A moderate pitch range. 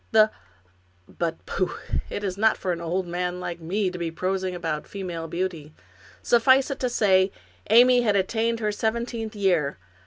Yes: average, 4.3 semitones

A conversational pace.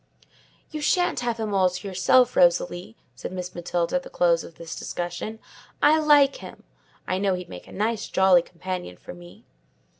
Yes: average, 180 wpm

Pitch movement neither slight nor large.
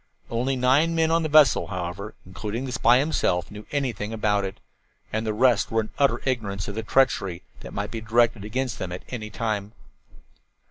Yes: average, 4.2 semitones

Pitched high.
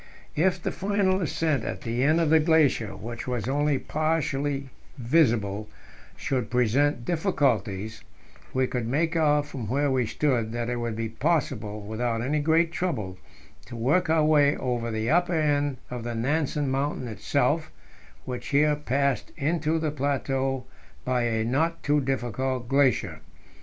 No: low, 135 Hz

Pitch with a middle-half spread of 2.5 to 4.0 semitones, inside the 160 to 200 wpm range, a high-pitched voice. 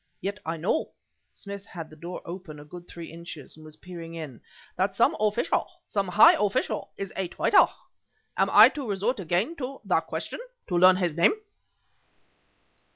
No: average, 3.3 semitones; average, 170 wpm; medium, 180 Hz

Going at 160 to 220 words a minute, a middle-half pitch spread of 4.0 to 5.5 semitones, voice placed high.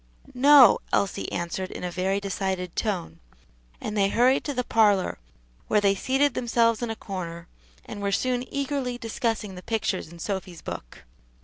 Yes: average, 165 wpm; average, 4.5 semitones; high, 205 Hz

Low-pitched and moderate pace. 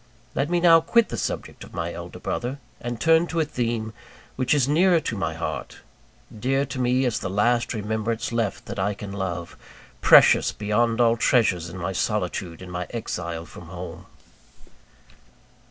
Yes: low, 115 Hz; average, 170 wpm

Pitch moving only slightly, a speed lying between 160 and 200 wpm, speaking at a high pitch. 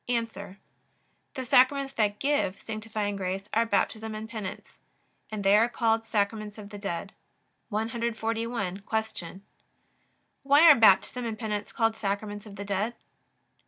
No: narrow, 2.3 semitones; slow, 135 wpm; high, 215 Hz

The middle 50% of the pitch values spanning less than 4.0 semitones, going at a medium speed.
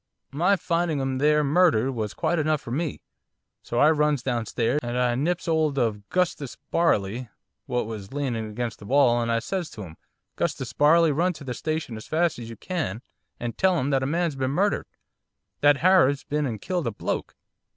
No: wide, 5.4 semitones; average, 195 wpm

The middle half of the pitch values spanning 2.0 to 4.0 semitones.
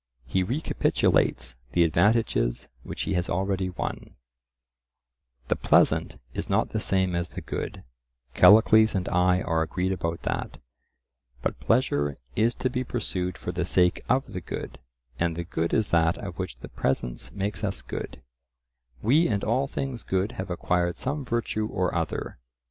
No: average, 4.6 semitones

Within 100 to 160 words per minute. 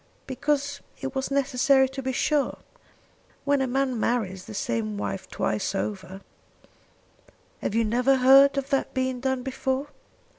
Yes: average, 150 wpm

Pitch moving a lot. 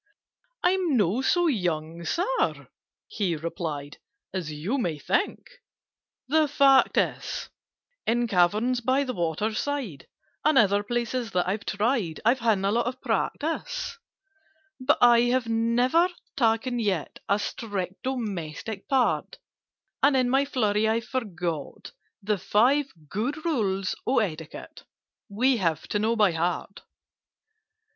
Yes: wide, 5.7 semitones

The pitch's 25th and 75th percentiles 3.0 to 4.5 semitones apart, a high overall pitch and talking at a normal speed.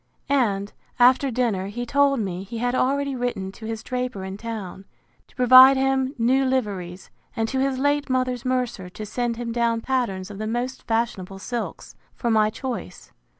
Yes: average, 3.8 semitones; high, 240 Hz; average, 175 wpm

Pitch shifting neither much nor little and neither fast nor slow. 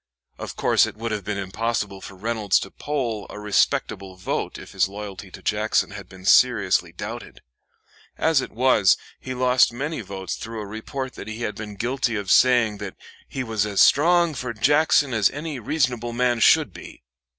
Yes: average, 4.0 semitones; average, 185 wpm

